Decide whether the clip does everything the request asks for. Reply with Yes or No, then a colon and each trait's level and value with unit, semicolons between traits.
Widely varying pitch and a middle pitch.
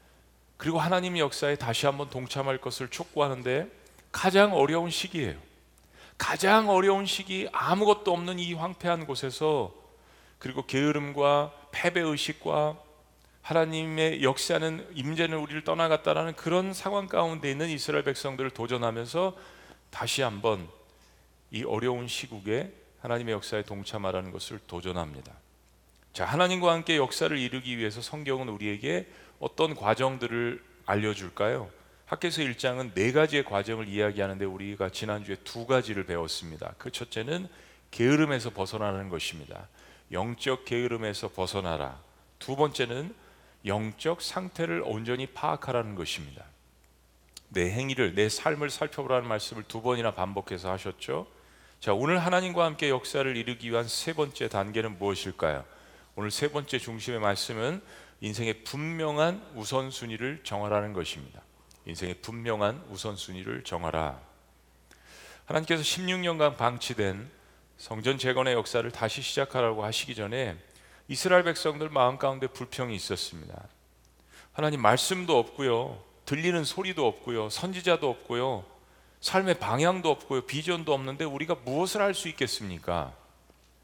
No: wide, 7.3 semitones; low, 125 Hz